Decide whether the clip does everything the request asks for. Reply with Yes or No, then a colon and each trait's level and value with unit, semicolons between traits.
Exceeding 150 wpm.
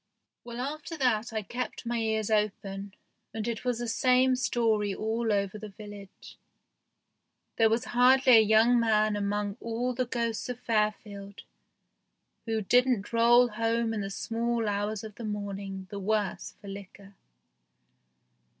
No: average, 145 wpm